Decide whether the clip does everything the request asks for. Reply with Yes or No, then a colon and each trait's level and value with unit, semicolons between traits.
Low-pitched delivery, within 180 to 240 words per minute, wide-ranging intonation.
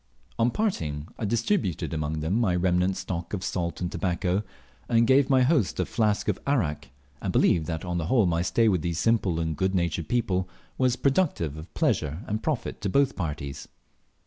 Yes: very low, 95 Hz; average, 190 wpm; wide, 5.9 semitones